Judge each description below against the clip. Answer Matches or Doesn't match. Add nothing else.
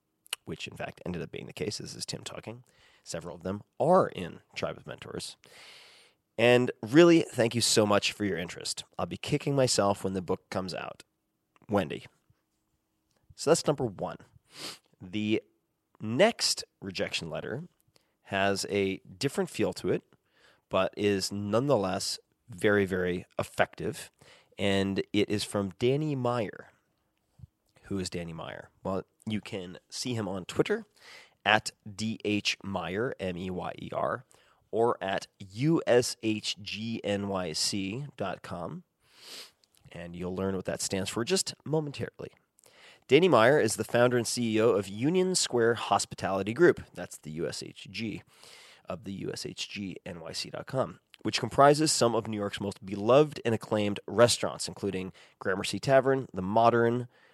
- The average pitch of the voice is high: Doesn't match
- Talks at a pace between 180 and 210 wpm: Doesn't match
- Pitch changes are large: Doesn't match